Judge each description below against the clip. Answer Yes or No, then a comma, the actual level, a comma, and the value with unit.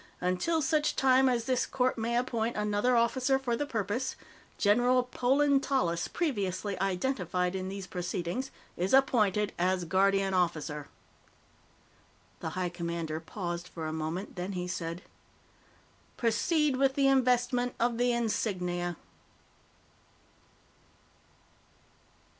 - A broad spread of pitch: Yes, wide, 6.0 semitones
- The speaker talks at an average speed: No, slow, 115 wpm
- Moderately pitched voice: No, high, 210 Hz